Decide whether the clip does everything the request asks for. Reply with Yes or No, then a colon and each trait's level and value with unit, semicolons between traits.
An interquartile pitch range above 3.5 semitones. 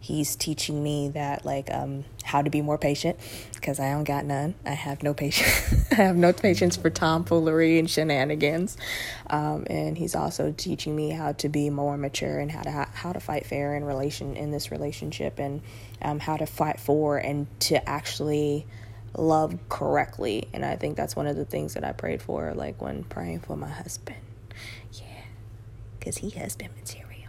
Yes: average, 5.2 semitones